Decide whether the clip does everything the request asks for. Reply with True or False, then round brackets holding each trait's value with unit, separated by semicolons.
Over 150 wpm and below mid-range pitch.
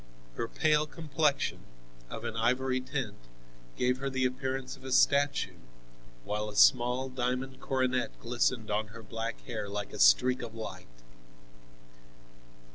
False (135 wpm; 125 Hz)